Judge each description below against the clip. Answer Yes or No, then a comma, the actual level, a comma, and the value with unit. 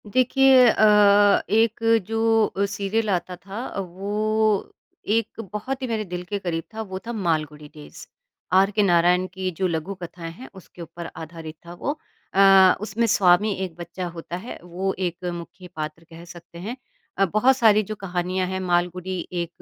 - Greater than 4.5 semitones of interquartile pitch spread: No, average, 3.6 semitones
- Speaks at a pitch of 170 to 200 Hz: Yes, high, 190 Hz